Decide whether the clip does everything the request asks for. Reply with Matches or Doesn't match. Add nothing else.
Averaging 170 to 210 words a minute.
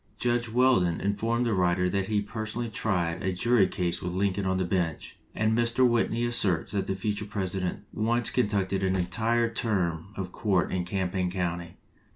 Matches